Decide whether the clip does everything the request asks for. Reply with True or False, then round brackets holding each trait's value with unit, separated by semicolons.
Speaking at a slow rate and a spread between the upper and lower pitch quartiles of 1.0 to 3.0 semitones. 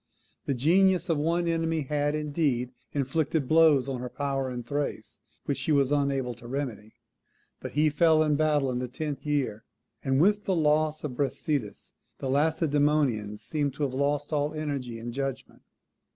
False (180 wpm; 2.7 semitones)